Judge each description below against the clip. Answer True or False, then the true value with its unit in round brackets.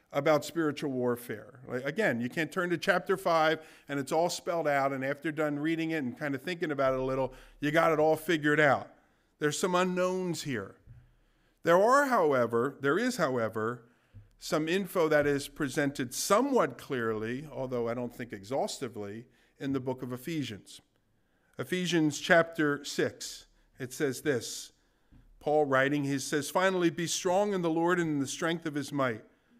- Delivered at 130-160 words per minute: False (170 wpm)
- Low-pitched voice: False (145 Hz)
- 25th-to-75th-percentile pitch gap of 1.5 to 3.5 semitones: False (4.2 semitones)